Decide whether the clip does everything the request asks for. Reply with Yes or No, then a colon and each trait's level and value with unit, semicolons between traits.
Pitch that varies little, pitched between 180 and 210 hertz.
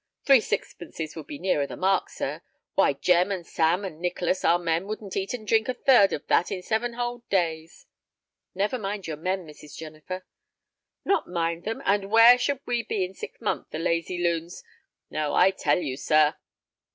No: average, 4.2 semitones; medium, 185 Hz